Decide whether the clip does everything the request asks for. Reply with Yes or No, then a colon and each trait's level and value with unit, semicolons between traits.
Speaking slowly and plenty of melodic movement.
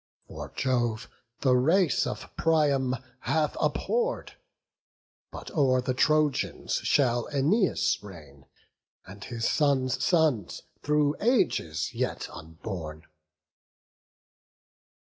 Yes: slow, 90 wpm; wide, 5.9 semitones